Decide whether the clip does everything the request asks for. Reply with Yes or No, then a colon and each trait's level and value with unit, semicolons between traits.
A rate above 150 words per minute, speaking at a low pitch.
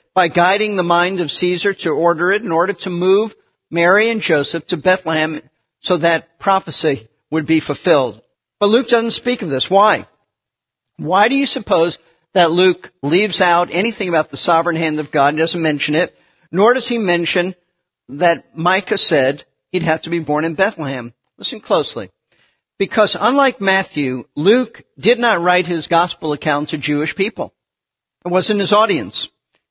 No: average, 170 wpm; medium, 175 Hz